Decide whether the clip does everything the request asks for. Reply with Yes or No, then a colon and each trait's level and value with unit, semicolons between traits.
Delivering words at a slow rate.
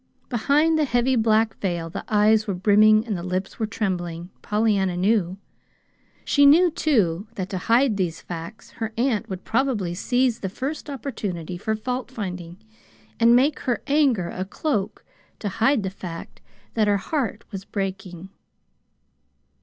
No: average, 150 wpm